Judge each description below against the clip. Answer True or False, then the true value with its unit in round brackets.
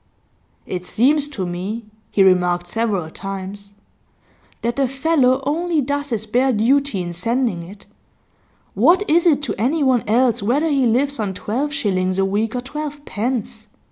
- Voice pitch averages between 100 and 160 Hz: False (235 Hz)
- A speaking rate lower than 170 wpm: True (155 wpm)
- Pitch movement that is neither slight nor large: False (6.1 semitones)